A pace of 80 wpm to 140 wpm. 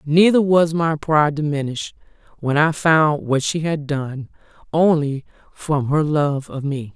No: average, 155 wpm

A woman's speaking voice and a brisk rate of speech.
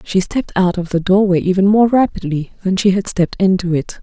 Yes: female; fast, 225 wpm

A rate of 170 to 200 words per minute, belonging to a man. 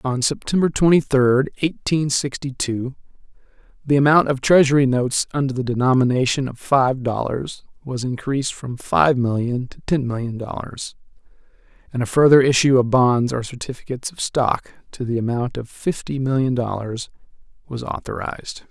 No: average, 150 wpm; male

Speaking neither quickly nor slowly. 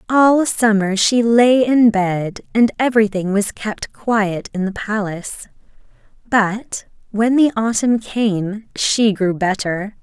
No: slow, 130 wpm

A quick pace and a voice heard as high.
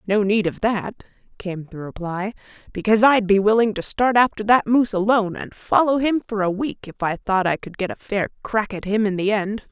Yes: fast, 230 wpm; high, 205 Hz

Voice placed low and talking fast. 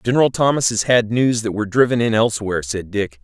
Yes: low, 115 Hz; fast, 225 wpm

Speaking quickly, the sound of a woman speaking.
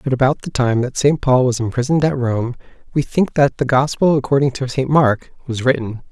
No: fast, 215 wpm; male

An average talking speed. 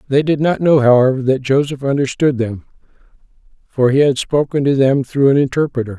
Yes: average, 180 wpm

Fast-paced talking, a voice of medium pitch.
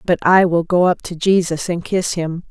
Yes: fast, 240 wpm; medium, 175 Hz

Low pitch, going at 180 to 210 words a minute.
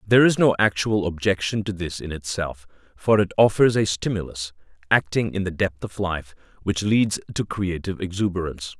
No: very low, 95 Hz; average, 170 wpm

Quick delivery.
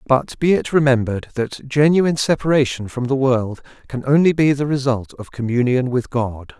No: average, 175 wpm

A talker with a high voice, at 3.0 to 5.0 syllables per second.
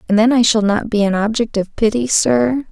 No: high, 225 Hz; 5.3 syllables/s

